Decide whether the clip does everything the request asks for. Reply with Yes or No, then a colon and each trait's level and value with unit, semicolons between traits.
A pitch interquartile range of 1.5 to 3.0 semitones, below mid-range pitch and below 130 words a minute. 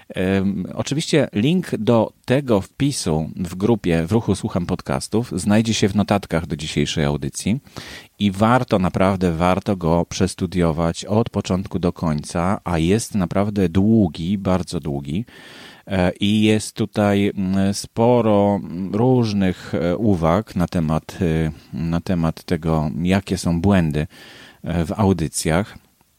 No: average, 3.7 semitones; very low, 95 Hz; average, 115 wpm